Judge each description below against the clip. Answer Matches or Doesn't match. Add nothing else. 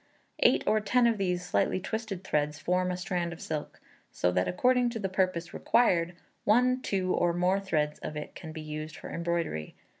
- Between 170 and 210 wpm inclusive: Matches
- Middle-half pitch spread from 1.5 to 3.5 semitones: Doesn't match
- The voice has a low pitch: Doesn't match